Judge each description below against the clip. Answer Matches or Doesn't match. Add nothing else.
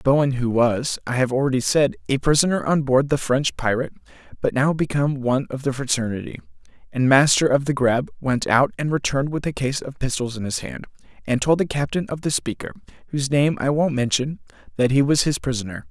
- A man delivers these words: Matches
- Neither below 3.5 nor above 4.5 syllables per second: Doesn't match